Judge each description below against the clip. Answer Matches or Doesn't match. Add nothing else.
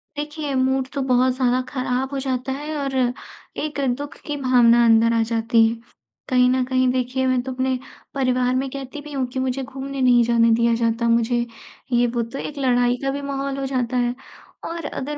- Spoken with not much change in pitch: Matches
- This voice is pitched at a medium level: Doesn't match